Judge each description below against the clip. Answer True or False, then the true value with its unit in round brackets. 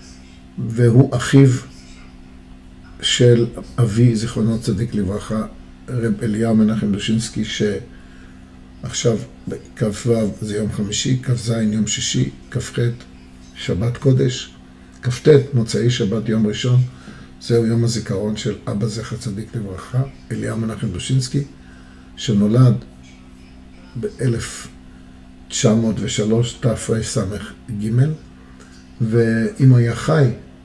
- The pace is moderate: False (90 wpm)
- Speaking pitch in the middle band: False (110 Hz)